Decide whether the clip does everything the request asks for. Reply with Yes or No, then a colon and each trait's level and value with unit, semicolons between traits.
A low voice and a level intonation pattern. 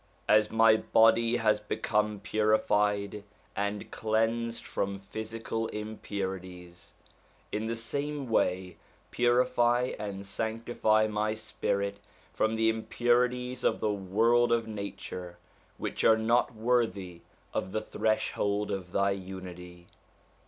Yes: low, 110 Hz; narrow, 2.3 semitones